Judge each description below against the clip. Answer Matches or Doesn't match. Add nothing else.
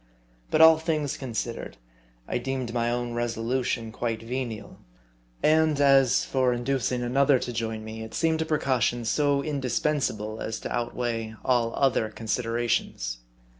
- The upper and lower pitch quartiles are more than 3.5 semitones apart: Doesn't match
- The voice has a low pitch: Matches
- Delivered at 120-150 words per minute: Matches